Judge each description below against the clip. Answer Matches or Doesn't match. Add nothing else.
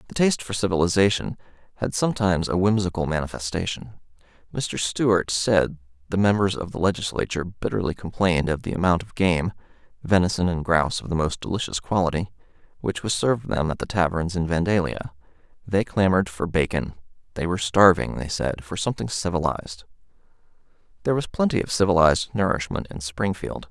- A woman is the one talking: Doesn't match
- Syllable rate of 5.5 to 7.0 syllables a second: Matches